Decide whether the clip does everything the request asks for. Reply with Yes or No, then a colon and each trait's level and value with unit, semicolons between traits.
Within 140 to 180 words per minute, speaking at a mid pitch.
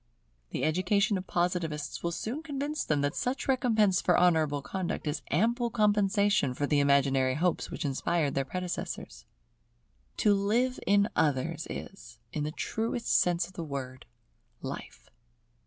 Yes: average, 145 wpm; medium, 180 Hz